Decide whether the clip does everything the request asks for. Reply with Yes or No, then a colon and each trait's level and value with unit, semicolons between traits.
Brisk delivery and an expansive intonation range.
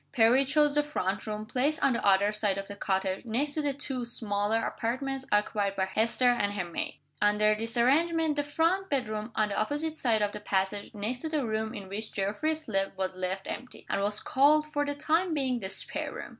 Yes: fast, 215 wpm; wide, 5.8 semitones